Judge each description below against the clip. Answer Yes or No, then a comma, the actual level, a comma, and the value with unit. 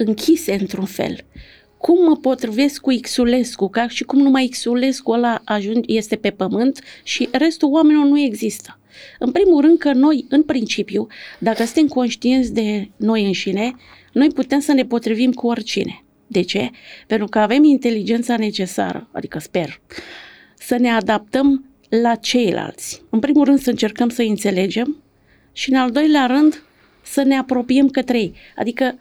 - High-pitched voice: Yes, high, 245 Hz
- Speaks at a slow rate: No, average, 155 wpm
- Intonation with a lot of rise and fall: No, average, 3.8 semitones